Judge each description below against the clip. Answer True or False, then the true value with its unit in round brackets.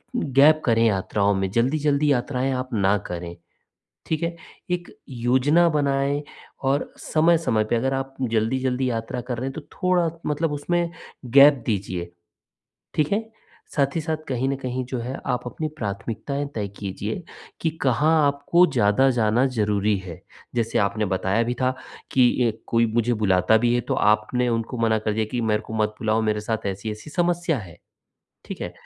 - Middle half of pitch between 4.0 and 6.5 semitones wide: True (4.7 semitones)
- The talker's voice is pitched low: True (125 Hz)